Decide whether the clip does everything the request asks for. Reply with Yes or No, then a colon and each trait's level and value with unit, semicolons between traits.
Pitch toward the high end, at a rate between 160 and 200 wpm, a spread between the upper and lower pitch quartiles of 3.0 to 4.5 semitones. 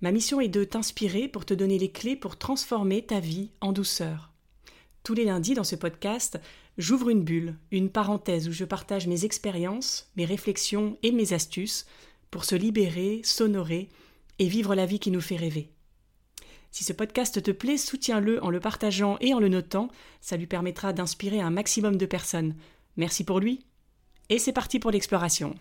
Yes: high, 200 Hz; average, 185 wpm; average, 3.5 semitones